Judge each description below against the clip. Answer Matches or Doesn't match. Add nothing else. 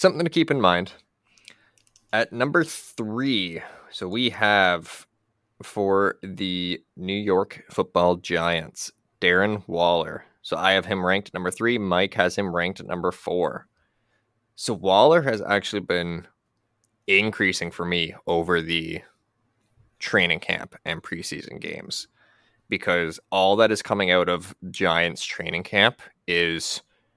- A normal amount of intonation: Matches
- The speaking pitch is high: Doesn't match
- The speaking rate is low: Matches